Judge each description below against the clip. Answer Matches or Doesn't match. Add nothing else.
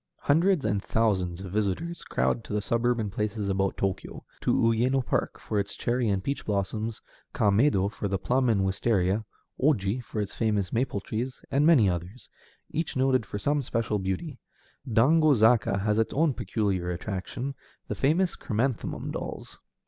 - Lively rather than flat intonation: Doesn't match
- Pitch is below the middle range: Matches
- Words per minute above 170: Doesn't match